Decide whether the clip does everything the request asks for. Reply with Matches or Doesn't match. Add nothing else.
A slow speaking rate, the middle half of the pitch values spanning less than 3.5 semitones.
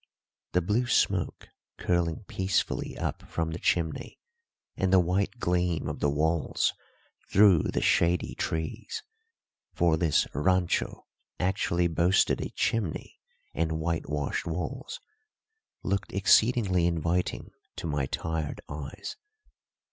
Matches